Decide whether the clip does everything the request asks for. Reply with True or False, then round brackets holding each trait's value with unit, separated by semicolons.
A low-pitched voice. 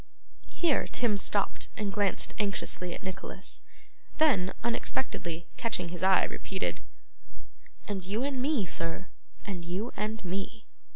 False (200 Hz)